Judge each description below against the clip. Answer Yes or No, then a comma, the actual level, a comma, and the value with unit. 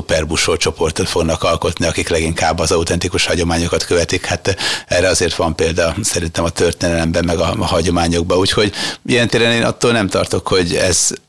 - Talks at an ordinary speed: No, fast, 160 wpm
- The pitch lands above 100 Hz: No, very low, 85 Hz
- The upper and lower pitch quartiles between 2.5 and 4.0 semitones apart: Yes, average, 2.8 semitones